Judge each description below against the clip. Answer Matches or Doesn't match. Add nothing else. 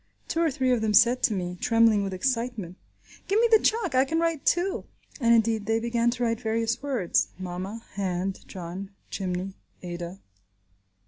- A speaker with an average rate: Matches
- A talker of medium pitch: Doesn't match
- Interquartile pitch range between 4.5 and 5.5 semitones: Matches